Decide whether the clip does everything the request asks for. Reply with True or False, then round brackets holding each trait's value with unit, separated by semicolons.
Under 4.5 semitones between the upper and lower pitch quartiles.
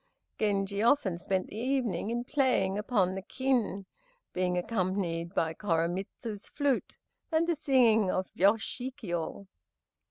False (5.0 semitones)